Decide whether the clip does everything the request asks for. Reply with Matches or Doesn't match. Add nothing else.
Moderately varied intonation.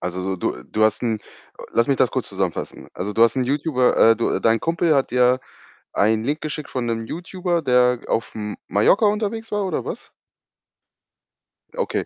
Doesn't match